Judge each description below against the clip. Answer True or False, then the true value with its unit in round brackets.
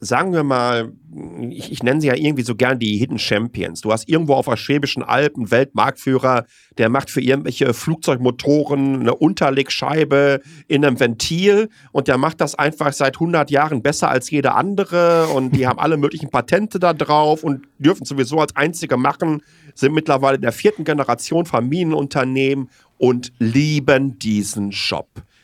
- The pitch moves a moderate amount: True (3.4 semitones)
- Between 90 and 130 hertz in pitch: False (140 Hz)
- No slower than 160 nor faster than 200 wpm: True (165 wpm)